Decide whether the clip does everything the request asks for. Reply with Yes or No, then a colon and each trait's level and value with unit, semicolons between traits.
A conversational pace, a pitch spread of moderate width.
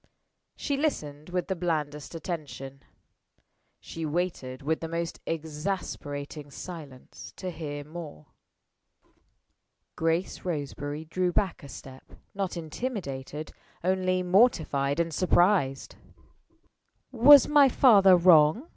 No: slow, 100 wpm; average, 4.0 semitones